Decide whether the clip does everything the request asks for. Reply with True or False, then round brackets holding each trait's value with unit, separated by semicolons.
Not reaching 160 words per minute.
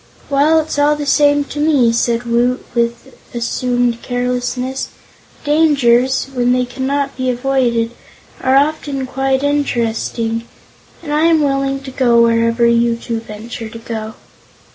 True (140 wpm)